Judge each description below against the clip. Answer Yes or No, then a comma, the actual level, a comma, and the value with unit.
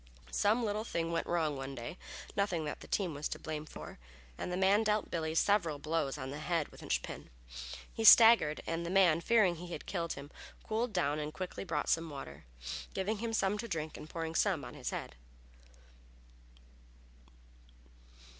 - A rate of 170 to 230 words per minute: Yes, average, 185 wpm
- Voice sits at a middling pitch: Yes, medium, 170 Hz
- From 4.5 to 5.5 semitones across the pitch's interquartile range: Yes, average, 4.8 semitones